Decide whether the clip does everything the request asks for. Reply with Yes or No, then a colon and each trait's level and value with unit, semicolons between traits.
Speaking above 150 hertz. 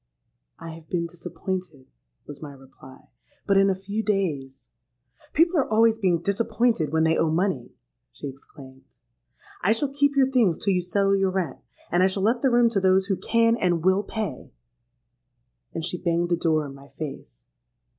Yes: medium, 185 Hz